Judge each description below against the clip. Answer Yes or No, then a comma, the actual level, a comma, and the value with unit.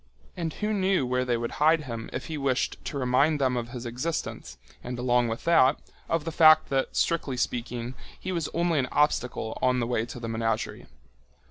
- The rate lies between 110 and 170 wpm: No, average, 200 wpm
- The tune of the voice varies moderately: Yes, average, 4.5 semitones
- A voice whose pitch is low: Yes, low, 130 Hz